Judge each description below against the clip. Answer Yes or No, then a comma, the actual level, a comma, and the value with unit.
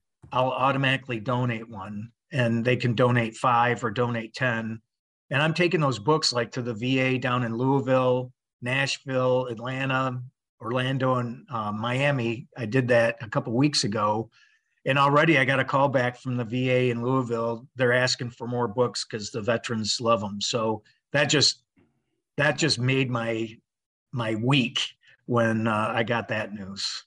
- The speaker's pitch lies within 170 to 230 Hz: No, low, 125 Hz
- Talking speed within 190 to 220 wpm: No, average, 165 wpm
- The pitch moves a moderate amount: No, narrow, 2.3 semitones